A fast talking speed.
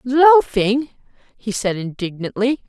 No: slow, 90 wpm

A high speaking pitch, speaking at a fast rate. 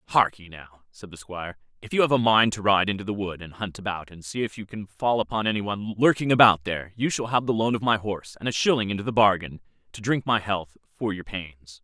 No: low, 105 Hz; fast, 260 wpm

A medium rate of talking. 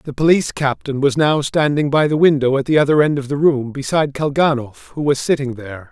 No: fast, 225 wpm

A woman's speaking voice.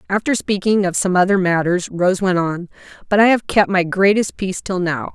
Yes: female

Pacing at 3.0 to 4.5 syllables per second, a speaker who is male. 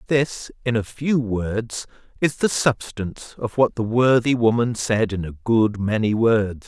Yes: 4.0 syllables/s; male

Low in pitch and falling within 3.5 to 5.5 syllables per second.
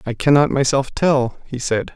Yes: low, 130 Hz; 4.5 syllables/s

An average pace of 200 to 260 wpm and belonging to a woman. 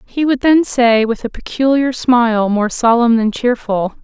No: average, 180 wpm; female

